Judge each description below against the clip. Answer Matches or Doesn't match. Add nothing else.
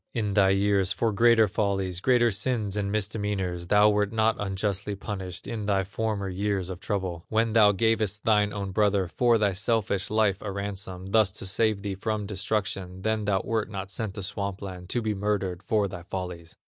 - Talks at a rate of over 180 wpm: Matches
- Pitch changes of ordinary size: Doesn't match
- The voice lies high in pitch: Doesn't match